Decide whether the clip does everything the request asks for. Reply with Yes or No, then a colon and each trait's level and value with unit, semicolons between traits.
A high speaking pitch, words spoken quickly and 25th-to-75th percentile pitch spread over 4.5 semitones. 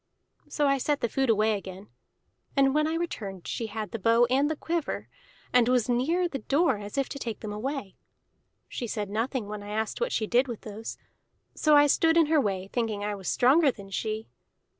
Yes: high, 240 Hz; fast, 210 wpm; average, 5.2 semitones